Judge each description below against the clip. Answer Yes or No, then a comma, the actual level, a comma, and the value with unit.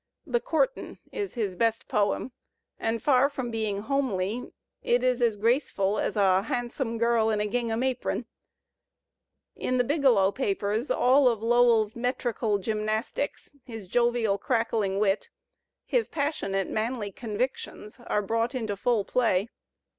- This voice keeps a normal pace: No, slow, 130 wpm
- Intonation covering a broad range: No, average, 3.2 semitones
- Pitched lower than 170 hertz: No, high, 230 Hz